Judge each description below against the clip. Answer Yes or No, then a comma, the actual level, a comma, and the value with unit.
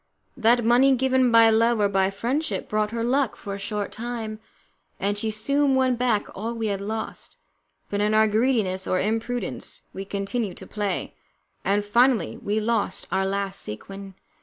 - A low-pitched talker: No, high, 220 Hz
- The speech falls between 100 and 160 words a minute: No, average, 170 wpm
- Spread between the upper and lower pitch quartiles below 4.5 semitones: Yes, average, 3.2 semitones